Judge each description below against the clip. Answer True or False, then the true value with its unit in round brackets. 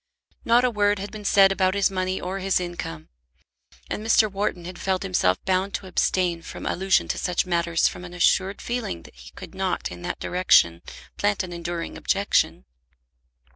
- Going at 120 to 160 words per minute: False (180 wpm)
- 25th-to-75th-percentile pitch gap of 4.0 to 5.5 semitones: False (2.4 semitones)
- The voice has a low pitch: False (185 Hz)